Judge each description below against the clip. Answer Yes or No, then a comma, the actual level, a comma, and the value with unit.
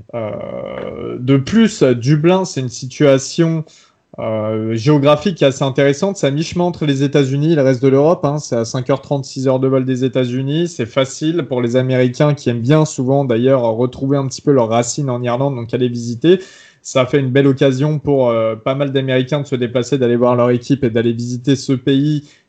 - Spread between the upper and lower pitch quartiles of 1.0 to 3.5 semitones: Yes, average, 2.9 semitones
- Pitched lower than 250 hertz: Yes, low, 135 Hz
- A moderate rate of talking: Yes, average, 195 wpm